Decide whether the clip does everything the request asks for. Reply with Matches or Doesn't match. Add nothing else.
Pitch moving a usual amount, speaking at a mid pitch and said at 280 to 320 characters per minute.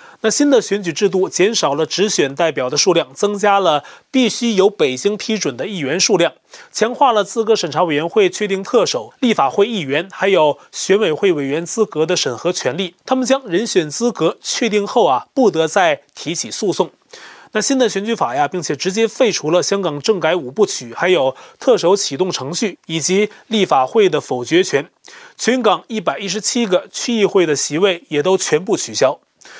Doesn't match